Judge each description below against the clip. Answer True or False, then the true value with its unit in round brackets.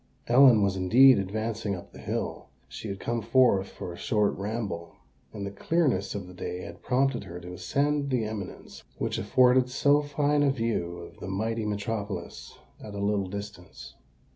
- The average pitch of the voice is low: True (105 Hz)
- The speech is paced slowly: False (175 wpm)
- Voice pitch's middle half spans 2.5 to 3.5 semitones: False (4.7 semitones)